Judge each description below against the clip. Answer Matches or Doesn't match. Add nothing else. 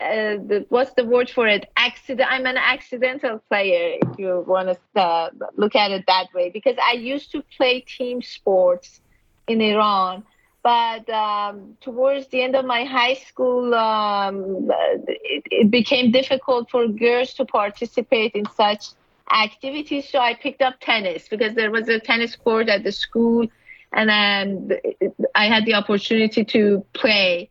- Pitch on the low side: Doesn't match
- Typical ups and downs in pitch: Matches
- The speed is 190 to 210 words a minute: Doesn't match